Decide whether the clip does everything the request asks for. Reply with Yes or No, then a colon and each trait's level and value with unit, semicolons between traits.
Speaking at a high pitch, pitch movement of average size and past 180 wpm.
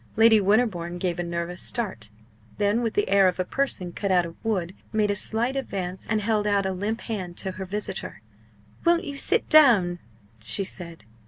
Yes: high, 200 Hz; average, 3.8 semitones; average, 190 wpm